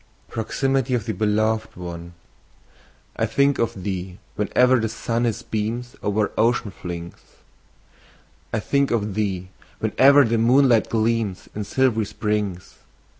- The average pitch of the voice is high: No, low, 110 Hz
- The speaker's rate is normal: No, slow, 125 wpm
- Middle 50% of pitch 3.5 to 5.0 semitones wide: No, average, 3.0 semitones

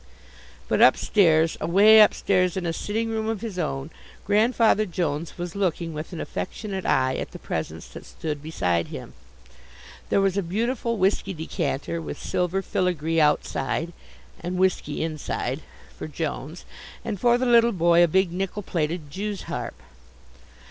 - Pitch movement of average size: Yes, average, 4.2 semitones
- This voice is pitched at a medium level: Yes, medium, 180 Hz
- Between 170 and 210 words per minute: No, average, 150 wpm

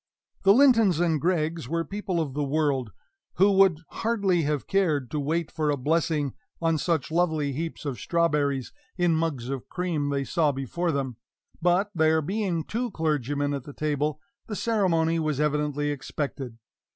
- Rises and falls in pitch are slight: No, average, 3.4 semitones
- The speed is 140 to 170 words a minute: Yes, average, 165 wpm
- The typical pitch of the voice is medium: Yes, medium, 155 Hz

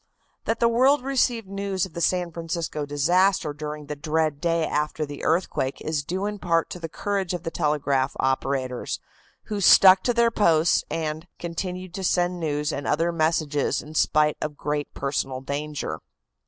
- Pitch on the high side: No, medium, 165 Hz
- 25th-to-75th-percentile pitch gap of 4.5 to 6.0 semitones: No, average, 3.9 semitones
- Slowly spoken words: No, average, 170 wpm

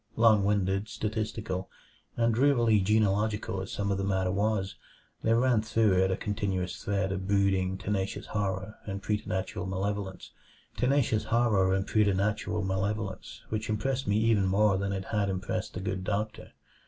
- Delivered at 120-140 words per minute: Yes, slow, 135 wpm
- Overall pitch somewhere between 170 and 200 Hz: No, low, 100 Hz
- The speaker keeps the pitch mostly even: Yes, narrow, 2.1 semitones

